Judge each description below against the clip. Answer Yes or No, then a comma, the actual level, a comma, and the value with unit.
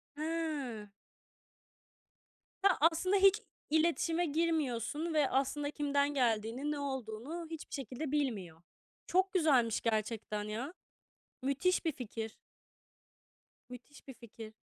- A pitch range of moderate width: No, wide, 5.7 semitones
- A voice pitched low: No, very high, 280 Hz